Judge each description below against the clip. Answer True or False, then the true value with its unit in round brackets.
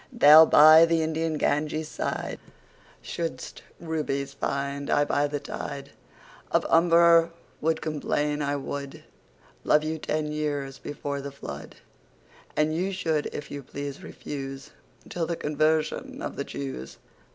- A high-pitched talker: False (150 Hz)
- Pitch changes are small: True (2.1 semitones)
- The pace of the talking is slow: True (120 wpm)